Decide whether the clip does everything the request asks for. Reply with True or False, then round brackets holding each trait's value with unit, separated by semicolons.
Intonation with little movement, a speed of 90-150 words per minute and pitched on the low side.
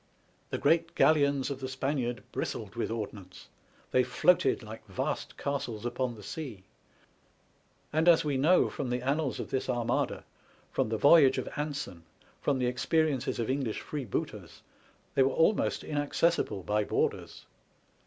False (4.0 semitones; 145 wpm; 130 Hz)